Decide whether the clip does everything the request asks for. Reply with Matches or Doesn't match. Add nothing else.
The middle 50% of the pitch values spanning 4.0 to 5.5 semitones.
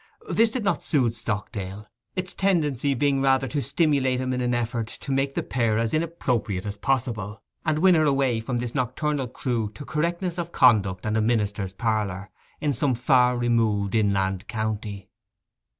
Matches